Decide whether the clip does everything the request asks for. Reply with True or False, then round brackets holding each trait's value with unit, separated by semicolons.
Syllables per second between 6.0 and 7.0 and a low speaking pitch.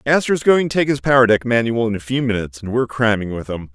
True (6.7 syllables/s; 120 Hz)